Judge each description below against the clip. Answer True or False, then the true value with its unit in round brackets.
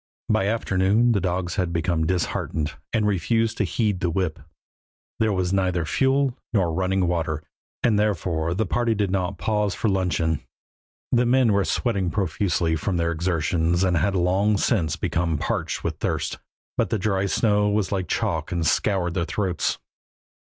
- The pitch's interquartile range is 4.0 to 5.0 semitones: False (3.4 semitones)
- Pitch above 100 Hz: False (95 Hz)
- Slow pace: False (165 wpm)